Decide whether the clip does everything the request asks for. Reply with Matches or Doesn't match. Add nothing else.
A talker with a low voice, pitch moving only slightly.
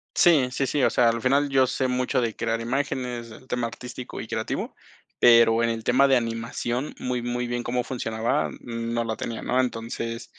Matches